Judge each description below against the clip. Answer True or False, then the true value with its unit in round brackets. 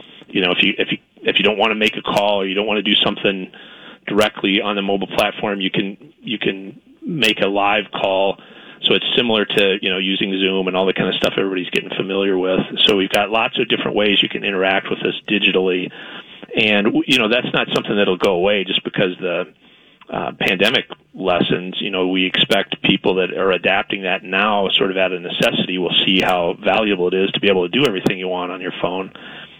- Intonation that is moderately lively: False (1.5 semitones)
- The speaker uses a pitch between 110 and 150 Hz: False (95 Hz)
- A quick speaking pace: True (225 wpm)